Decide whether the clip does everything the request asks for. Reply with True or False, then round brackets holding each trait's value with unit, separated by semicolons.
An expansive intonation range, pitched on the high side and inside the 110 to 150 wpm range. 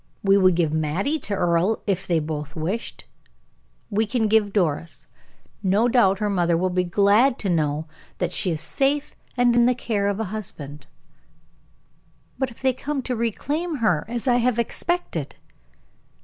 False (5.7 semitones; 200 Hz; 165 wpm)